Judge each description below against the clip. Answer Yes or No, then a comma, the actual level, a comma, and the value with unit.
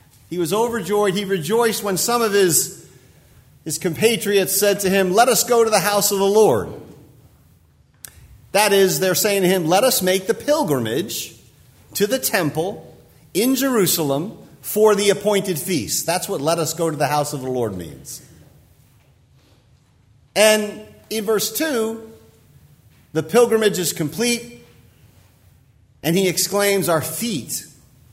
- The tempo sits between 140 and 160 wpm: Yes, average, 145 wpm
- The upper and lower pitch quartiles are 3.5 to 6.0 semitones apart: Yes, average, 4.8 semitones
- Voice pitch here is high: Yes, high, 195 Hz